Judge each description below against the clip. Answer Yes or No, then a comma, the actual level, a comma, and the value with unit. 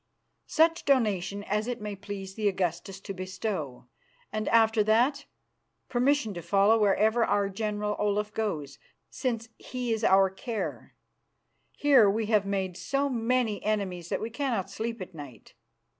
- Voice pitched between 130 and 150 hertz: No, high, 210 Hz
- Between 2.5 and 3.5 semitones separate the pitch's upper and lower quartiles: Yes, average, 3.0 semitones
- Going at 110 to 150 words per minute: Yes, average, 145 wpm